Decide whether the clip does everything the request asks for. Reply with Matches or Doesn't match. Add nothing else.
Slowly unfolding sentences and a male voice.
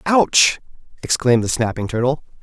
Matches